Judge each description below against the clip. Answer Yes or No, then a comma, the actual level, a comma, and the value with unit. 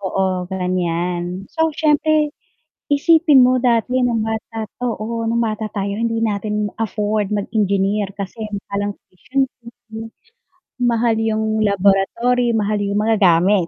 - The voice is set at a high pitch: Yes, high, 215 Hz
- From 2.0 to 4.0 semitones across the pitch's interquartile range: Yes, average, 2.8 semitones